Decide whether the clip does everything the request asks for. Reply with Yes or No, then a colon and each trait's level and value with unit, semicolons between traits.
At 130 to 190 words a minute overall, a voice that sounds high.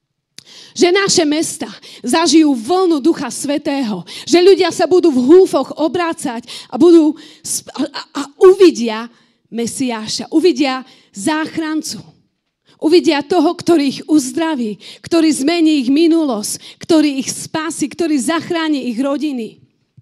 No: average, 115 wpm; very high, 305 Hz